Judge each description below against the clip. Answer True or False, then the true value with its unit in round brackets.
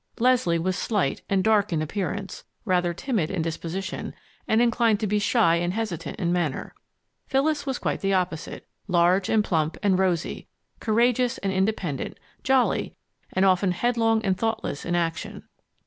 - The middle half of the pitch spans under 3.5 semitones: False (4.3 semitones)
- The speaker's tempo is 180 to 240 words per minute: False (155 wpm)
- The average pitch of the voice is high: True (195 Hz)